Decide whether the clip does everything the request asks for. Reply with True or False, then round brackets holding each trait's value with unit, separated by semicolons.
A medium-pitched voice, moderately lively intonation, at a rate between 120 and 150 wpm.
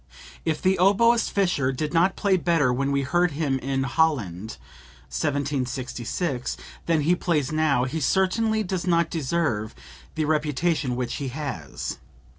True (150 Hz; 4.9 semitones; 140 wpm)